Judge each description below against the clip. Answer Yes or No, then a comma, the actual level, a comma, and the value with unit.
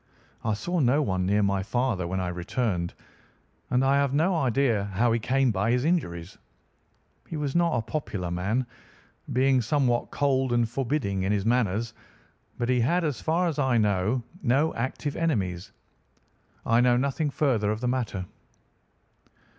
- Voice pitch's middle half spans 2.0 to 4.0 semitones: No, average, 5.3 semitones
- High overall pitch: No, low, 120 Hz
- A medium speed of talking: Yes, average, 160 wpm